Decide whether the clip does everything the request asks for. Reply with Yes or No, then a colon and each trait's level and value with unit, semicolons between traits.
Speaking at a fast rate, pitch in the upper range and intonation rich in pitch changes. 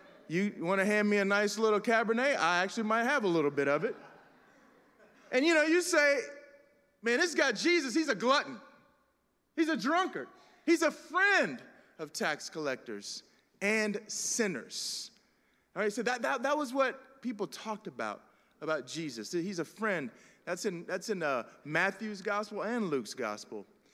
No: average, 170 wpm; high, 225 Hz; wide, 6.0 semitones